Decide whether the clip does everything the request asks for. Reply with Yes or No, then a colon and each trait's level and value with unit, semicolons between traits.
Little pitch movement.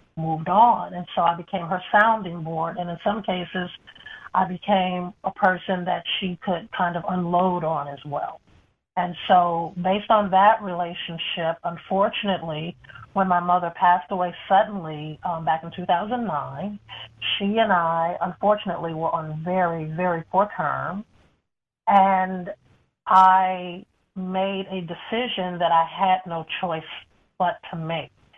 Yes: narrow, 2.3 semitones